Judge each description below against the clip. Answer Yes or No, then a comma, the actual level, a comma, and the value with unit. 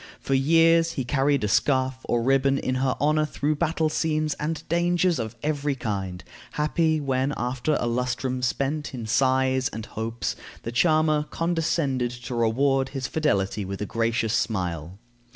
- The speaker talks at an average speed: Yes, average, 160 wpm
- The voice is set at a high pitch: No, low, 135 Hz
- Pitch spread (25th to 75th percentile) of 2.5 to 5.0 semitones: Yes, average, 4.5 semitones